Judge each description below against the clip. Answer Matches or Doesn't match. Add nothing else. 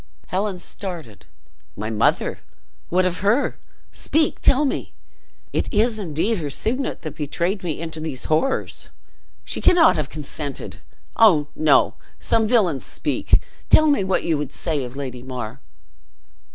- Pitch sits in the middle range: Matches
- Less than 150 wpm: Matches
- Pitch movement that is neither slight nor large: Doesn't match